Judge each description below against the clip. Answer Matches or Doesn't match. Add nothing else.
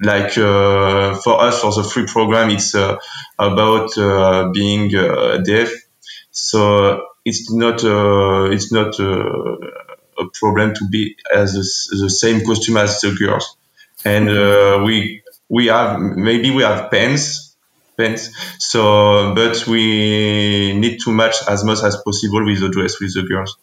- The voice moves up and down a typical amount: Doesn't match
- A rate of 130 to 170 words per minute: Matches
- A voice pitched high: Doesn't match